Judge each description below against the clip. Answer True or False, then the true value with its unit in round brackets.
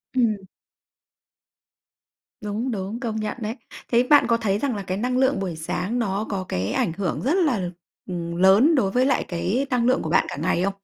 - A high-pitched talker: True (210 Hz)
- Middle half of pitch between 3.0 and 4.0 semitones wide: False (4.8 semitones)